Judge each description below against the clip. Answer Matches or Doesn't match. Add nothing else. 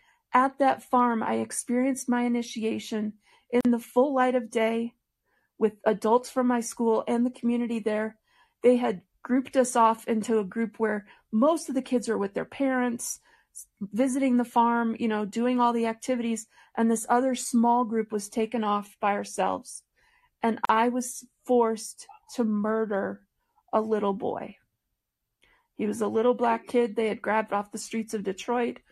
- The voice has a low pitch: Doesn't match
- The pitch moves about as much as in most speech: Doesn't match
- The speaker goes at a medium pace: Matches